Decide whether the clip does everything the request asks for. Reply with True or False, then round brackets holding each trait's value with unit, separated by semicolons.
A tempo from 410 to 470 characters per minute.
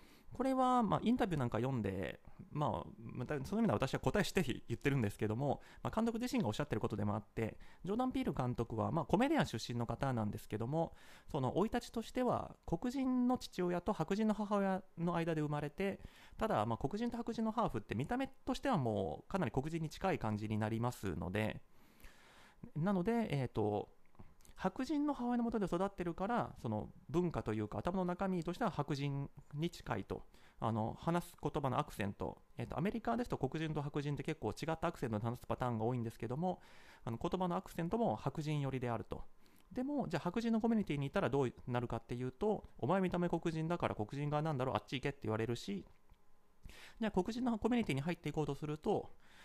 True (435 characters per minute)